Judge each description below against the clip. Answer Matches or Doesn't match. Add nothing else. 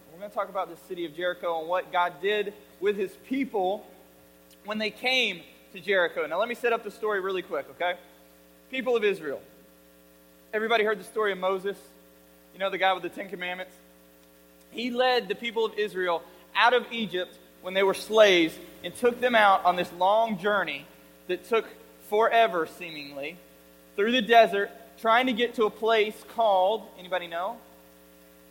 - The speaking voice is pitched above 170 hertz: Matches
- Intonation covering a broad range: Matches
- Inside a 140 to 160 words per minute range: Doesn't match